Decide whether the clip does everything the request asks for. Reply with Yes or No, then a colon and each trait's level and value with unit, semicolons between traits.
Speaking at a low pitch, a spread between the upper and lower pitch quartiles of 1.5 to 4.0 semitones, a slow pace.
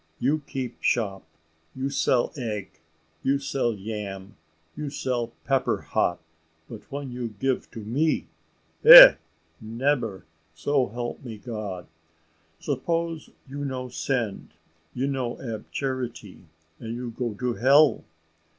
Yes: low, 125 Hz; average, 3.7 semitones; slow, 125 wpm